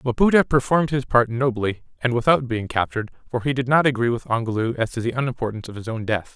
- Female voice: No, male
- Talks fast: Yes, fast, 215 wpm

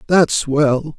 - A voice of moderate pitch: Yes, medium, 150 Hz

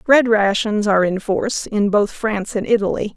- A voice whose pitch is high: Yes, high, 210 Hz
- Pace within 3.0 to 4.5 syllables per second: No, 5.1 syllables/s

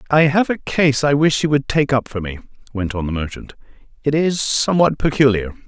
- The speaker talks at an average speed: No, fast, 210 wpm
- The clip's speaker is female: No, male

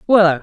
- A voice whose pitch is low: No, medium, 185 Hz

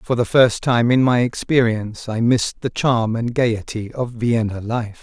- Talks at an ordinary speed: Yes, average, 190 wpm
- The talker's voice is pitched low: Yes, low, 115 Hz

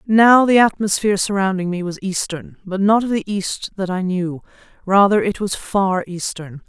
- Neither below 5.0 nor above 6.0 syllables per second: No, 4.7 syllables/s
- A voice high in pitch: Yes, high, 195 Hz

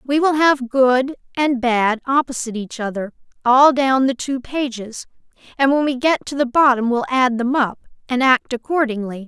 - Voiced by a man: No, female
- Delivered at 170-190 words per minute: Yes, average, 180 wpm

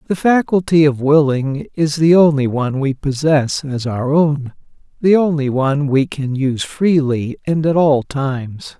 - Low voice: No, medium, 145 Hz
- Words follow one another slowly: No, average, 165 wpm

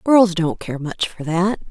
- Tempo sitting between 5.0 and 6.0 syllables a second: No, 4.0 syllables/s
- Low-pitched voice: No, medium, 180 Hz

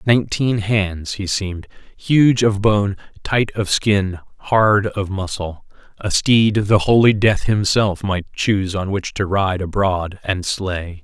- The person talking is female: No, male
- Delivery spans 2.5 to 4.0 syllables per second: Yes, 3.7 syllables/s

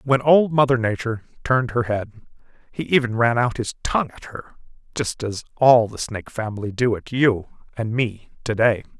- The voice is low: Yes, low, 120 Hz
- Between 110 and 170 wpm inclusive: No, average, 185 wpm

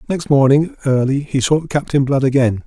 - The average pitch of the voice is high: No, medium, 140 Hz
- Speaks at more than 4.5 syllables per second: Yes, 5.0 syllables/s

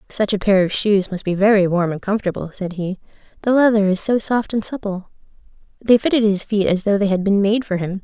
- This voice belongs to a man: No, female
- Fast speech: Yes, fast, 240 wpm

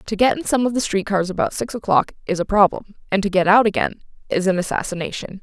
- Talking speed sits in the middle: No, fast, 245 wpm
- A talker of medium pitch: No, high, 200 Hz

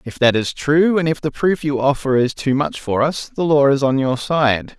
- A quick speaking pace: Yes, fast, 265 wpm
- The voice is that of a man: Yes, male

